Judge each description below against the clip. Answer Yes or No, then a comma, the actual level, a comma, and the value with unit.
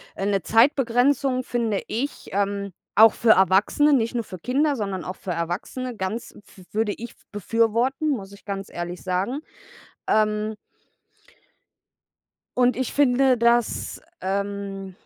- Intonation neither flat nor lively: Yes, average, 4.1 semitones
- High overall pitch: Yes, high, 220 Hz